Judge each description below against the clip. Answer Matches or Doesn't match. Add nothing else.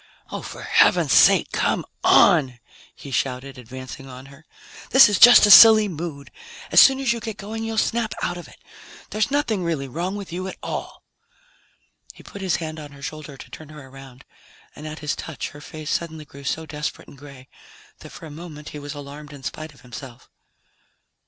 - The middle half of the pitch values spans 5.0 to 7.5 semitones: Matches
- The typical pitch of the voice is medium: Matches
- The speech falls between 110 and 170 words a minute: Doesn't match